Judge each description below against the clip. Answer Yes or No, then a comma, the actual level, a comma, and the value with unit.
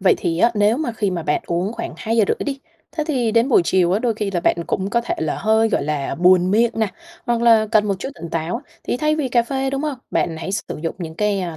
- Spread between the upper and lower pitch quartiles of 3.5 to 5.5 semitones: Yes, average, 4.9 semitones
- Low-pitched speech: No, high, 215 Hz